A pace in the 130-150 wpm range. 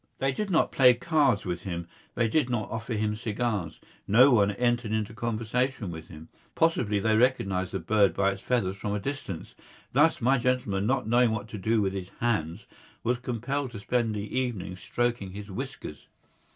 No: average, 185 wpm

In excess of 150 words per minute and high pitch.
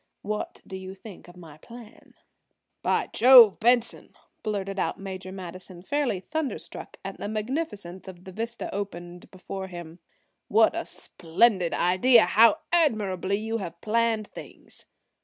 No: average, 140 wpm; high, 200 Hz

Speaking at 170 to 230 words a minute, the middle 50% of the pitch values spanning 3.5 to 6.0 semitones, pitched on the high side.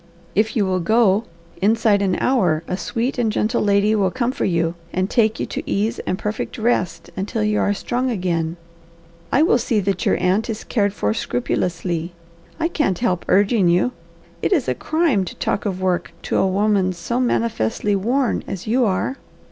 Yes: average, 190 wpm; average, 4.0 semitones; high, 205 Hz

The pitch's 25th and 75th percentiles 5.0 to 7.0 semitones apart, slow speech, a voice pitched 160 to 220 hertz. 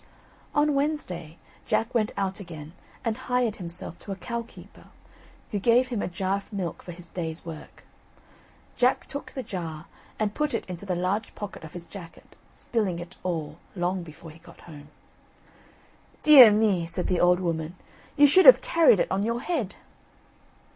No: wide, 5.4 semitones; average, 175 wpm; high, 190 Hz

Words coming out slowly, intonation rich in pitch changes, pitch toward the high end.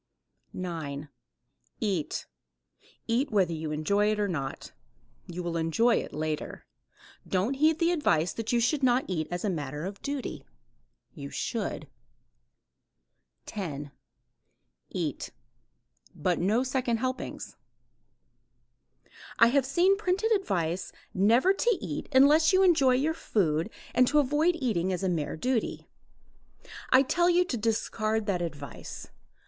Yes: slow, 130 wpm; wide, 8.3 semitones; high, 220 Hz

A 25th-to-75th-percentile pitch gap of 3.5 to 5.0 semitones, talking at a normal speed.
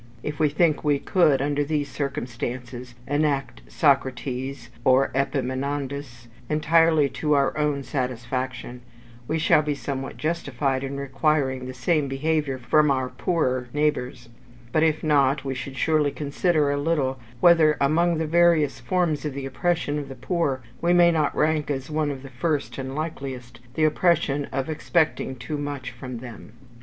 No: average, 2.8 semitones; average, 155 wpm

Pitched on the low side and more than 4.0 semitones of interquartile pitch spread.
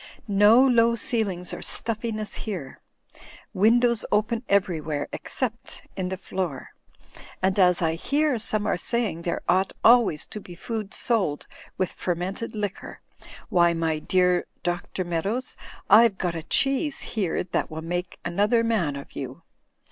No: high, 190 Hz; average, 4.8 semitones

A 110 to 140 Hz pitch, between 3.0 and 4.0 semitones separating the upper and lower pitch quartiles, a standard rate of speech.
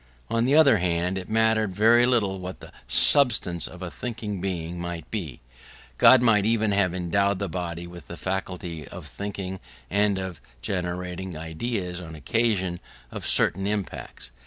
No: very low, 95 Hz; average, 3.5 semitones; average, 160 wpm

